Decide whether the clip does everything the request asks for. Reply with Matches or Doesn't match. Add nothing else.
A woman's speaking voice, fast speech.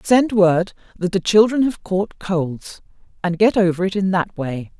Doesn't match